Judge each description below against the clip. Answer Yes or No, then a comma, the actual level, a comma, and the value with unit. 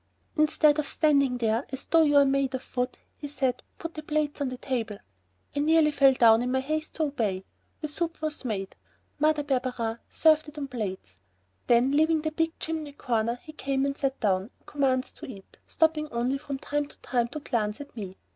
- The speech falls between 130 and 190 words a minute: No, fast, 205 wpm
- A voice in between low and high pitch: No, very high, 275 Hz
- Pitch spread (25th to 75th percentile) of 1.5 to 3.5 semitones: No, average, 4.0 semitones